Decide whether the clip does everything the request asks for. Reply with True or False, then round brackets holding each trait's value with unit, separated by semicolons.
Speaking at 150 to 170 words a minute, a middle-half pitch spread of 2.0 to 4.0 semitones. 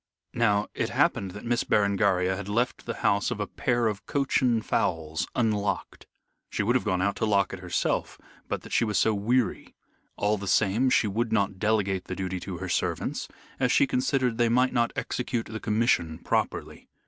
False (190 wpm; 3.4 semitones)